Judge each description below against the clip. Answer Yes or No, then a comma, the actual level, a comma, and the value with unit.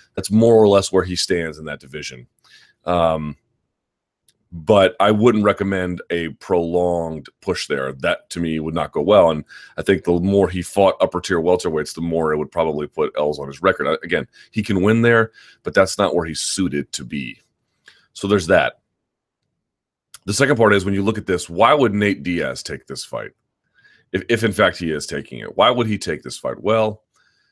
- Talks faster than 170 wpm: Yes, fast, 205 wpm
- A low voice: Yes, very low, 90 Hz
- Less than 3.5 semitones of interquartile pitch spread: No, average, 4.0 semitones